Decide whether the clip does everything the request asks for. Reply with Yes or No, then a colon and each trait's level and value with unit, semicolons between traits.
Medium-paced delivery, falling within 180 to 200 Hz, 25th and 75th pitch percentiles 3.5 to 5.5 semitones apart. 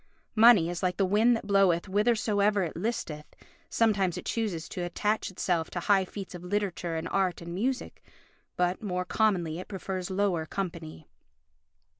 No: average, 160 wpm; high, 190 Hz; average, 2.9 semitones